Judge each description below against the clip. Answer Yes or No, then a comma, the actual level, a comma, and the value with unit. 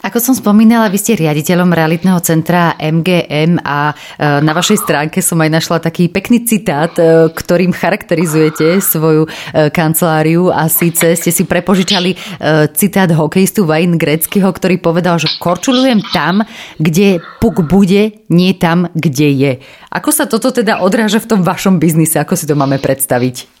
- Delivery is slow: No, average, 145 wpm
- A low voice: No, medium, 175 Hz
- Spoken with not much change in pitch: No, average, 3.4 semitones